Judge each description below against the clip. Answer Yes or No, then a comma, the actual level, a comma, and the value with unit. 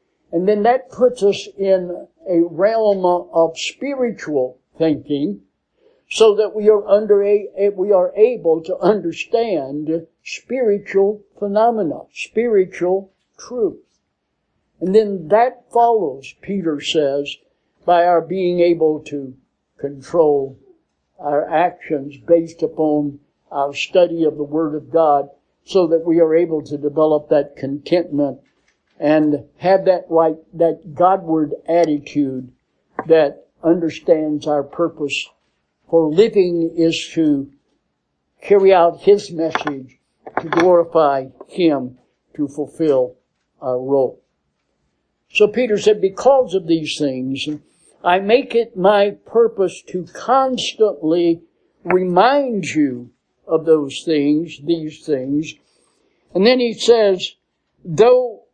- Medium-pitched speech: Yes, medium, 170 Hz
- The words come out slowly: Yes, slow, 115 wpm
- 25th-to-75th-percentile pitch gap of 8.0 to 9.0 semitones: No, average, 5.3 semitones